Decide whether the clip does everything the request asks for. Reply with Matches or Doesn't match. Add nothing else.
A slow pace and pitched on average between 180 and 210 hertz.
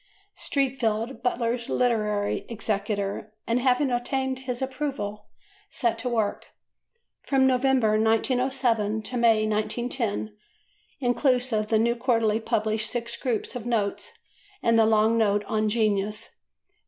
Doesn't match